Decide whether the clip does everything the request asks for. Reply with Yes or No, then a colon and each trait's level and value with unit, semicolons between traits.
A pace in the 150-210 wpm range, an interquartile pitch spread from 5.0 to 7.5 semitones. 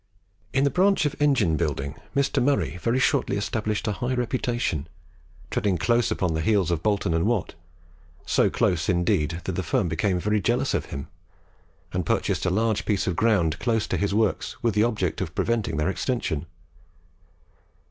Yes: average, 175 wpm; wide, 5.5 semitones